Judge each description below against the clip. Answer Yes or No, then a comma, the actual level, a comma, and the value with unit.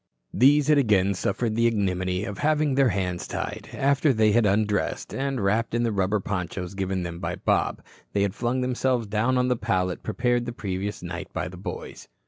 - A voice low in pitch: Yes, low, 105 Hz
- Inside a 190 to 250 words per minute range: Yes, average, 195 wpm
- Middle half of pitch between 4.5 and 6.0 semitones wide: Yes, average, 4.8 semitones